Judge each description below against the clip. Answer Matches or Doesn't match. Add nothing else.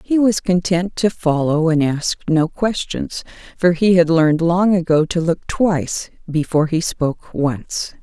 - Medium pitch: Matches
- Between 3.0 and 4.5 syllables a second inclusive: Matches